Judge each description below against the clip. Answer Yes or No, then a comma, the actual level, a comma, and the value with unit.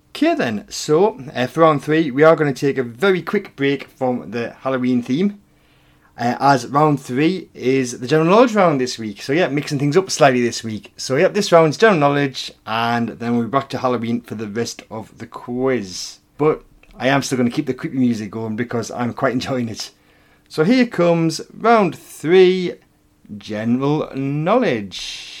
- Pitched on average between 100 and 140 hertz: Yes, low, 135 Hz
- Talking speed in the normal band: Yes, average, 190 wpm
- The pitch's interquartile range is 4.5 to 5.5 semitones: Yes, average, 5.2 semitones